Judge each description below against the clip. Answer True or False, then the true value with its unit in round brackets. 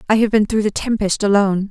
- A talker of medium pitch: False (210 Hz)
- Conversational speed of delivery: False (245 wpm)